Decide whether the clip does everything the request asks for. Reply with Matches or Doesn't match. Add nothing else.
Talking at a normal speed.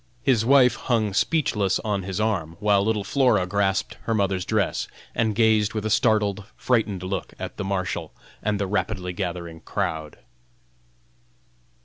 Matches